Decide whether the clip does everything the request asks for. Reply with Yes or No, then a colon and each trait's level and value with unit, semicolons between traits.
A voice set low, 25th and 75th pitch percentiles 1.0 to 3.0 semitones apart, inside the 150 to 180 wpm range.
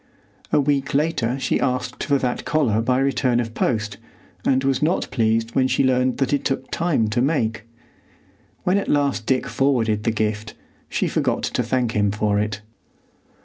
No: low, 125 Hz; average, 3.7 semitones; average, 175 wpm